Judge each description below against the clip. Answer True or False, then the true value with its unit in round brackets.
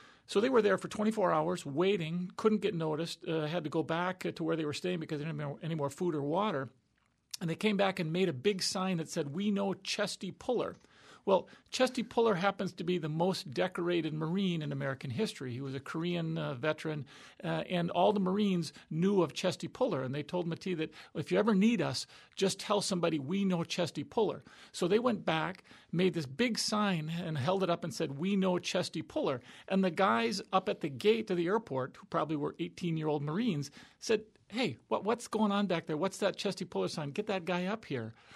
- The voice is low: False (180 Hz)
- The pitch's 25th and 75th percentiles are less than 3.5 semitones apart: False (3.8 semitones)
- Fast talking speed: True (225 wpm)